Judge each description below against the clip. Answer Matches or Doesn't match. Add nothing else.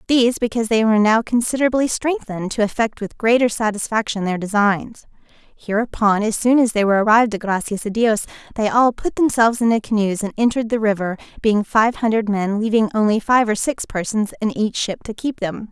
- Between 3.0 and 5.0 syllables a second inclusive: Doesn't match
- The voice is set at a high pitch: Matches